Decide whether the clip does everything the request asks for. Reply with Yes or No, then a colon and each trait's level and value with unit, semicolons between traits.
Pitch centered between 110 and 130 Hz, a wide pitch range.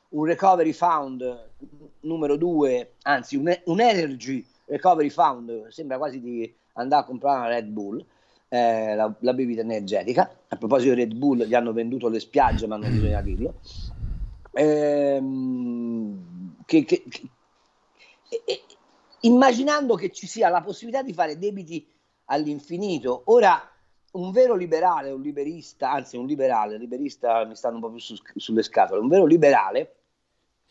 No: medium, 140 Hz; wide, 7.2 semitones